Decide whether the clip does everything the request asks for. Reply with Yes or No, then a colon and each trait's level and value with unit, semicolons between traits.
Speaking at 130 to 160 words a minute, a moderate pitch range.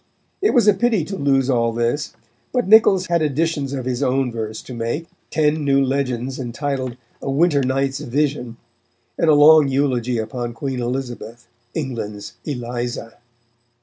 Yes: average, 150 wpm; average, 3.7 semitones